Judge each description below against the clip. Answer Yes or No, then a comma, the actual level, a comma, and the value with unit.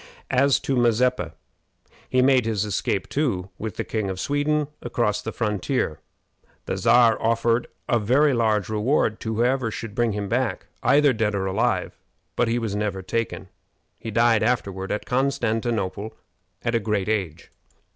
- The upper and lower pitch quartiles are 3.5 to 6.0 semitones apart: No, average, 3.0 semitones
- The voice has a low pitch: Yes, low, 115 Hz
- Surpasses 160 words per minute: No, average, 155 wpm